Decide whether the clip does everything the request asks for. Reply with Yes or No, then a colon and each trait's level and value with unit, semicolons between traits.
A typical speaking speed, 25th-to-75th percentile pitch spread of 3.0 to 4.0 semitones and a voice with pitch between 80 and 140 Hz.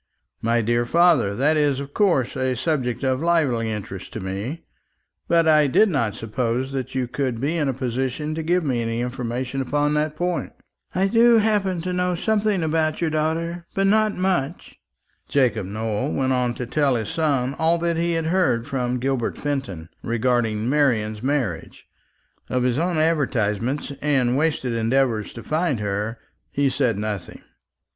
No: average, 165 wpm; wide, 5.4 semitones; low, 135 Hz